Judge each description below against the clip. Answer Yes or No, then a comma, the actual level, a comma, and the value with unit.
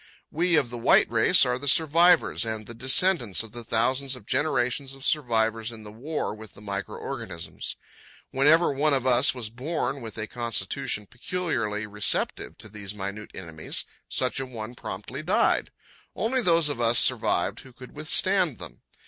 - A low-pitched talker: Yes, low, 120 Hz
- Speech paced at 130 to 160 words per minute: No, average, 170 wpm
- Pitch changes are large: No, average, 4.6 semitones